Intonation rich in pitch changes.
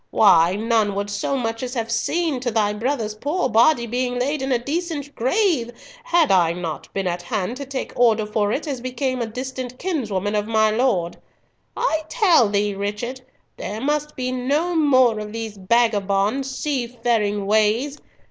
No: average, 4.5 semitones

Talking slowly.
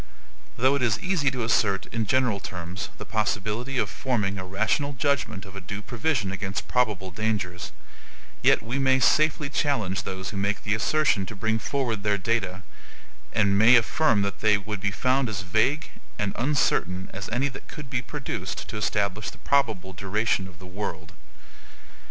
No: average, 175 wpm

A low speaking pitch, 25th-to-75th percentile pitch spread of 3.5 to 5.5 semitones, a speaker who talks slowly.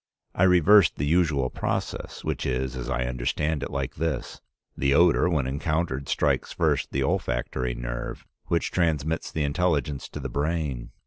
No: very low, 70 Hz; average, 4.1 semitones; average, 155 wpm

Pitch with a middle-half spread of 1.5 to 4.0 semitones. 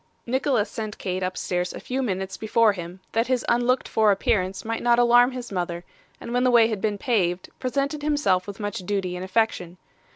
No: average, 4.6 semitones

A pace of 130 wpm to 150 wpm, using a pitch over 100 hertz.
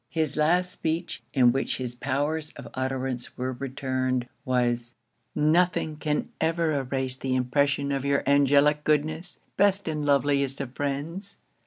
Yes: average, 140 wpm; medium, 140 Hz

